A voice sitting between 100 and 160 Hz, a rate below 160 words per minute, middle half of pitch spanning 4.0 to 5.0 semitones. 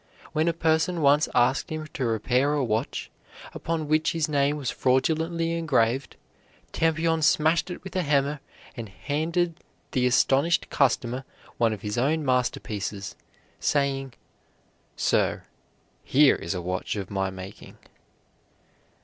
Yes: medium, 140 Hz; slow, 135 wpm; average, 4.7 semitones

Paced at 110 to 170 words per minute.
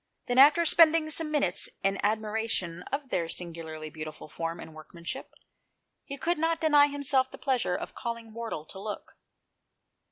Yes: average, 155 wpm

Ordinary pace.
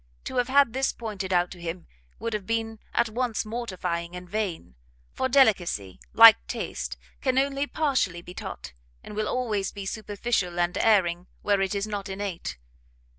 Yes: average, 170 wpm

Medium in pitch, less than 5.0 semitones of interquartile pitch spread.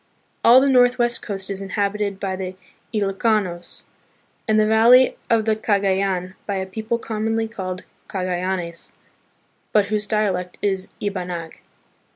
No: high, 200 Hz; average, 2.7 semitones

